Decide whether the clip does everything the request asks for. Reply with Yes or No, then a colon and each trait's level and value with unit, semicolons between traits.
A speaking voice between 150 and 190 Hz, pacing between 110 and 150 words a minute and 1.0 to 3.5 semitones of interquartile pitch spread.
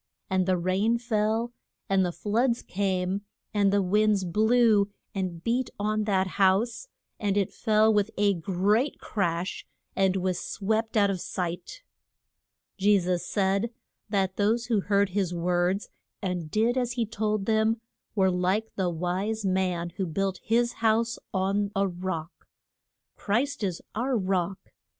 No: high, 200 Hz; average, 145 wpm; average, 2.8 semitones